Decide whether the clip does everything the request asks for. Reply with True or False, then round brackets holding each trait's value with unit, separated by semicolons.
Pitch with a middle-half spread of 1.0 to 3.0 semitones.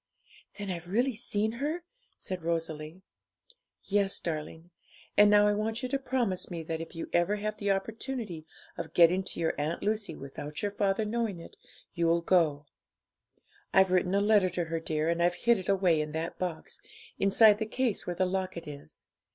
False (4.0 semitones)